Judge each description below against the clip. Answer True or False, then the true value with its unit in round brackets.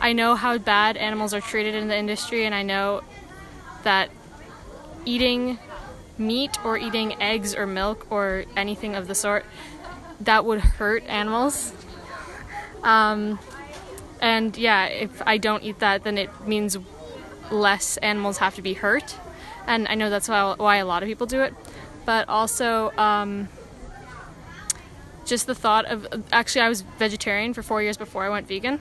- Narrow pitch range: True (1.8 semitones)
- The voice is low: False (215 Hz)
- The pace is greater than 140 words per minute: True (160 wpm)